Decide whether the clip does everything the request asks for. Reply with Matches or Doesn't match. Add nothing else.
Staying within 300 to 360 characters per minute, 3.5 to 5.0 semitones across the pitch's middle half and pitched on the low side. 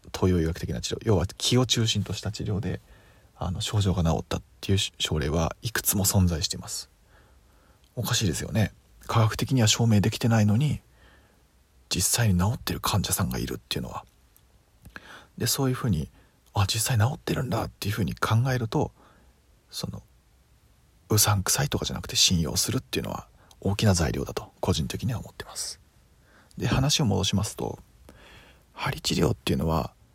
Matches